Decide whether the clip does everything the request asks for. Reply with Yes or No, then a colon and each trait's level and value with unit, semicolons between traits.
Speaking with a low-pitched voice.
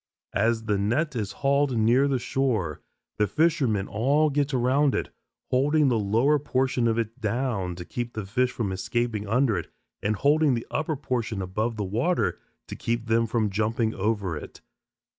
Yes: low, 115 Hz